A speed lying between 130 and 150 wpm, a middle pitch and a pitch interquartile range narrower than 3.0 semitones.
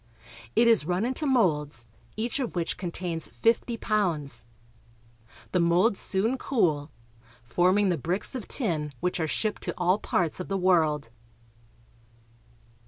No: slow, 135 wpm; medium, 180 Hz; average, 5.2 semitones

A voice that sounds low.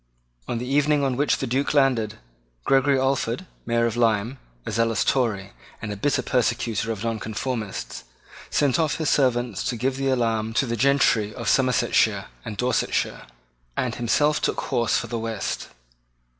Yes: low, 120 Hz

